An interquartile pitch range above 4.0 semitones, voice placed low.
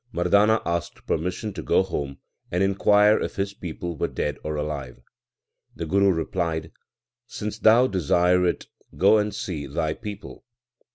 Yes: average, 4.4 semitones; very low, 90 Hz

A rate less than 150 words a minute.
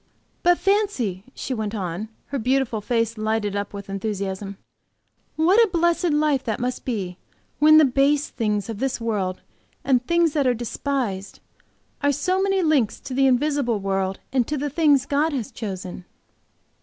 No: average, 165 wpm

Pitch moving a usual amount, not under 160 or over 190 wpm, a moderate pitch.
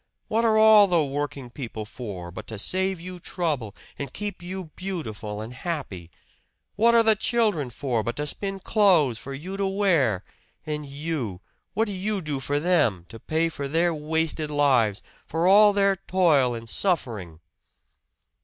No: wide, 7.4 semitones; average, 165 wpm; medium, 155 Hz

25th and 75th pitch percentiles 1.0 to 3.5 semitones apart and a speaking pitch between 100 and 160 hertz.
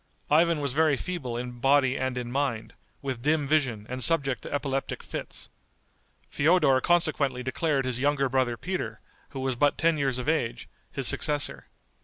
Yes: average, 3.0 semitones; low, 135 Hz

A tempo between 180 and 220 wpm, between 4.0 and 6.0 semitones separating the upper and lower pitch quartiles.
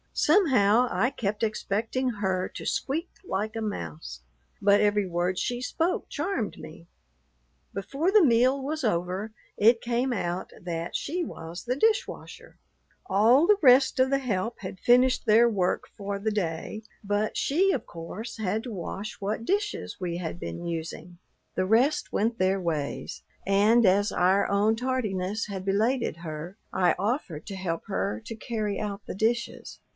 No: average, 160 wpm; average, 5.0 semitones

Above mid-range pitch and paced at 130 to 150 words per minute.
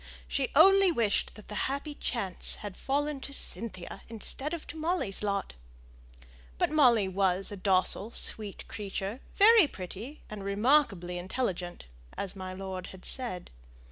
Yes: high, 210 Hz; average, 140 wpm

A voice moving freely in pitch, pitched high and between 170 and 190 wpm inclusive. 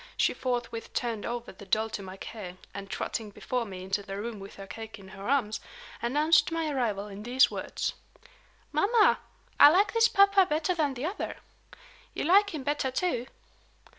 Yes: wide, 7.1 semitones; high, 240 Hz; average, 180 wpm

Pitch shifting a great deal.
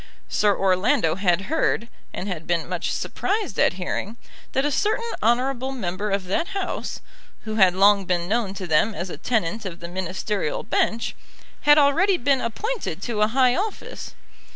Yes: wide, 6.5 semitones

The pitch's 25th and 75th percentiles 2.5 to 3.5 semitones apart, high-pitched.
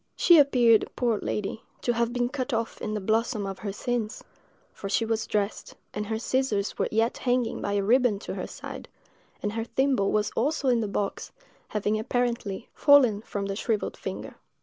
Yes: average, 2.9 semitones; high, 225 Hz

